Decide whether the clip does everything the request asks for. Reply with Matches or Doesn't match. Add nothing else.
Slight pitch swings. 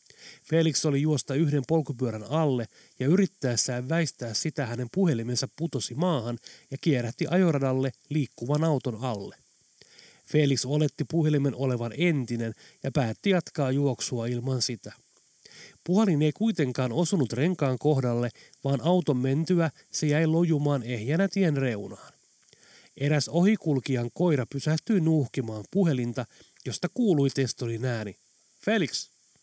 Doesn't match